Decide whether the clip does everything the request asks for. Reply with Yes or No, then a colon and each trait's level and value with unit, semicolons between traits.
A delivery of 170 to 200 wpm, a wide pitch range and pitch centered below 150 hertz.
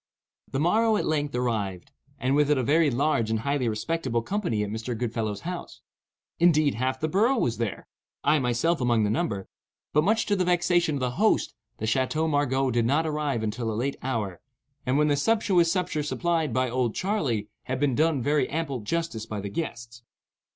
Yes: average, 185 wpm; wide, 5.8 semitones; low, 135 Hz